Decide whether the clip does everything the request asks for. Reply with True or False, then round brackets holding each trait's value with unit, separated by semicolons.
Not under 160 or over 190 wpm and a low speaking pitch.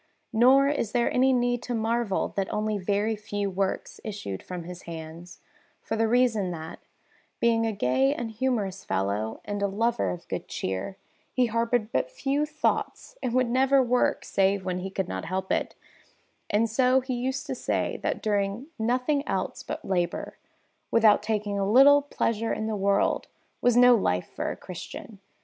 False (175 wpm; 220 Hz)